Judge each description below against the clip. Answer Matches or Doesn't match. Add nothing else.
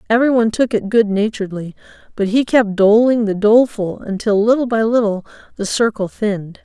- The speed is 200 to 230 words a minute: Doesn't match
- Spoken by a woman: Matches